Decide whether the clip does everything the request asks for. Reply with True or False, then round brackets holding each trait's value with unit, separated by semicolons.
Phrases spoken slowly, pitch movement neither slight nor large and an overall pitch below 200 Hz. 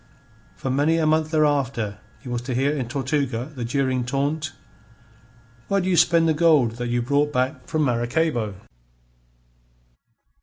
False (150 wpm; 4.2 semitones; 140 Hz)